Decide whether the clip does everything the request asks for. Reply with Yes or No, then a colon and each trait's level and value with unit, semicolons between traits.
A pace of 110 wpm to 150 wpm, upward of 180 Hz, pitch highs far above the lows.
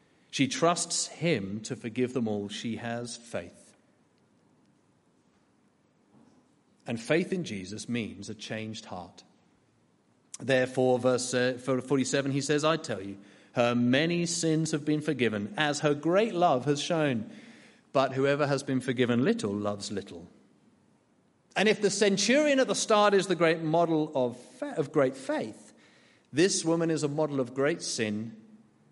No: average, 140 wpm; low, 135 Hz; wide, 5.7 semitones